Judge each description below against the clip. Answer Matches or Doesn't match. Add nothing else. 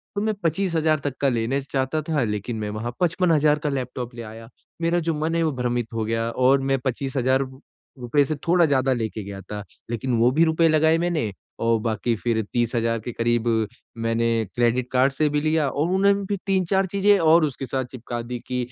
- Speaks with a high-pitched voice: Doesn't match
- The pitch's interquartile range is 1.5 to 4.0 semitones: Doesn't match